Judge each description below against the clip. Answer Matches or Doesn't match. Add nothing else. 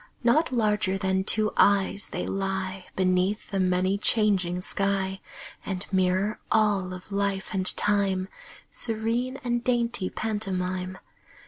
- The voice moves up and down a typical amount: Doesn't match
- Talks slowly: Matches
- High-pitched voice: Matches